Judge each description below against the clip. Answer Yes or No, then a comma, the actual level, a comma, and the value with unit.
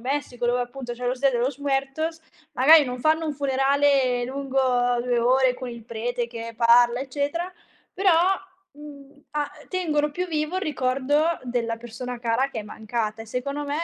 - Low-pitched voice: No, very high, 265 Hz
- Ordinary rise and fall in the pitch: Yes, average, 3.2 semitones